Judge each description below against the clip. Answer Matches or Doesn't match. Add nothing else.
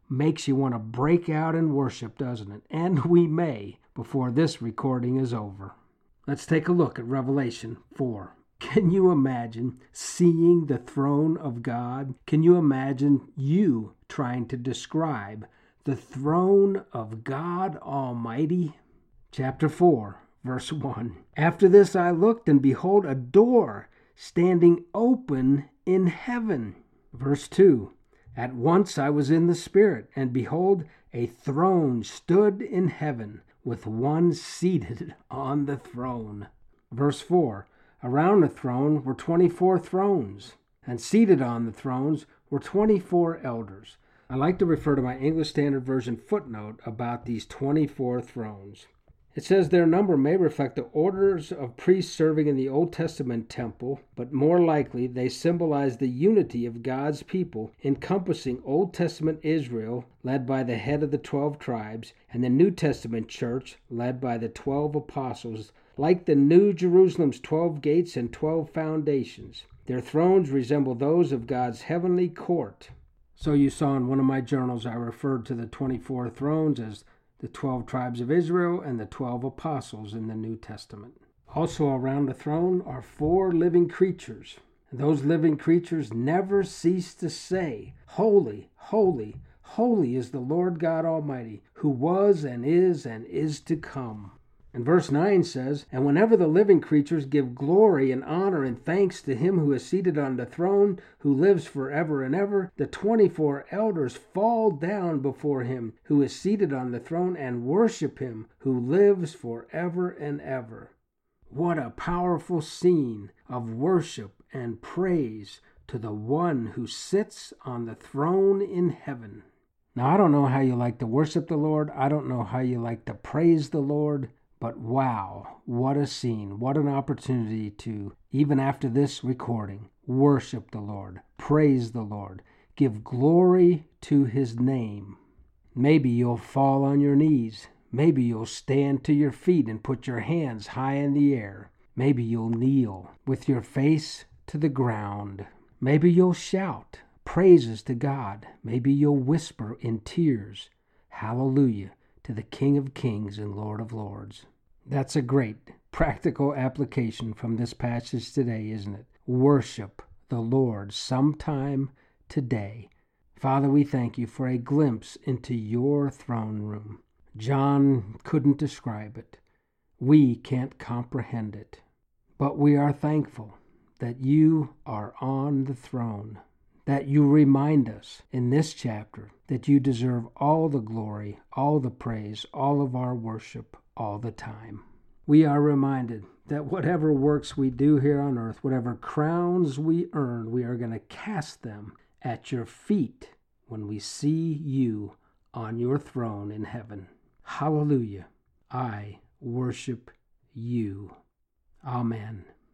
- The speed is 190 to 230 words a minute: Doesn't match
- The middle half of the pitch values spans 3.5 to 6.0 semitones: Matches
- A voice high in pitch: Doesn't match